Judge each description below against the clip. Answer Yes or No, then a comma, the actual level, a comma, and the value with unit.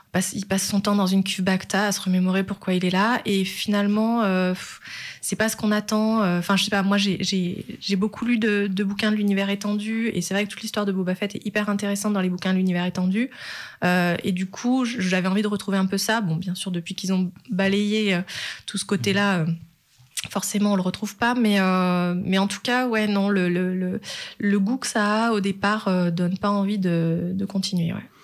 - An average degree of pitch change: No, narrow, 2.0 semitones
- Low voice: No, high, 195 Hz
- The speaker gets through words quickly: Yes, fast, 235 wpm